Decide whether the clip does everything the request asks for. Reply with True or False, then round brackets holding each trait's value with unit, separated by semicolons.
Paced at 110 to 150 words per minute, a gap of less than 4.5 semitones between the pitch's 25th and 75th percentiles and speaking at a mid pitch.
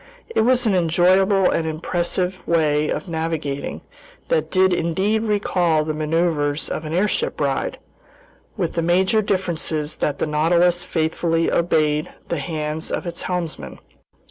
True (140 wpm; 2.9 semitones; 170 Hz)